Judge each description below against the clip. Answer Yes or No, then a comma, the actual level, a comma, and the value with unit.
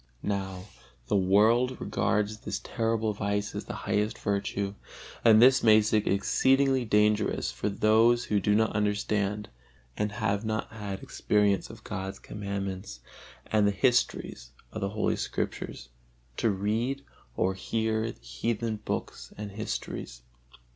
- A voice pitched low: Yes, low, 105 Hz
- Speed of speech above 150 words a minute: No, slow, 135 wpm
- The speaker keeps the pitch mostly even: Yes, narrow, 1.8 semitones